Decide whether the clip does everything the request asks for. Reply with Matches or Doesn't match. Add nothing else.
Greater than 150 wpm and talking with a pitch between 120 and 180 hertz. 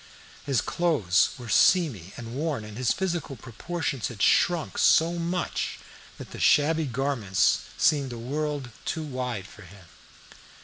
Doesn't match